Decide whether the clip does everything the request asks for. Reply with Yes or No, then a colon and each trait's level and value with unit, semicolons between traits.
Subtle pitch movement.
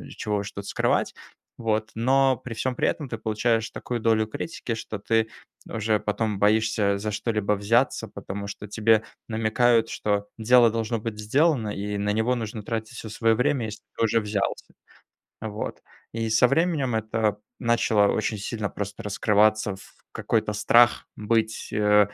Yes: narrow, 1.7 semitones